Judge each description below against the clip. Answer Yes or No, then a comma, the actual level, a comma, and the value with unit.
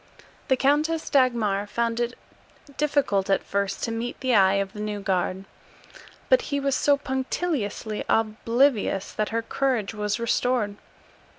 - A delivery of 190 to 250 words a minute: No, average, 140 wpm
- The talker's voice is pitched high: Yes, high, 230 Hz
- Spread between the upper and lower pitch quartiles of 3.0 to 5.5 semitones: Yes, average, 4.6 semitones